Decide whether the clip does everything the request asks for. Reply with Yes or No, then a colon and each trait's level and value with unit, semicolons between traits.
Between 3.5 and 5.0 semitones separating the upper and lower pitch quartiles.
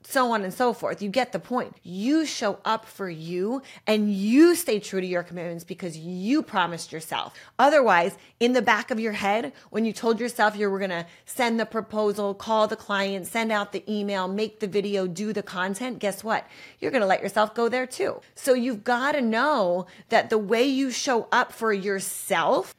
Yes: average, 3.8 semitones